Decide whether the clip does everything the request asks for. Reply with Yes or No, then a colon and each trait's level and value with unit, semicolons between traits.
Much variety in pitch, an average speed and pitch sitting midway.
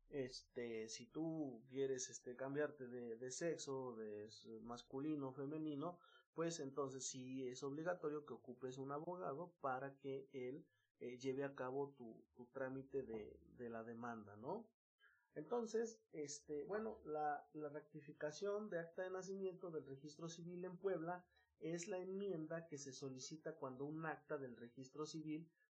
No: average, 4.1 semitones; average, 150 wpm; medium, 145 Hz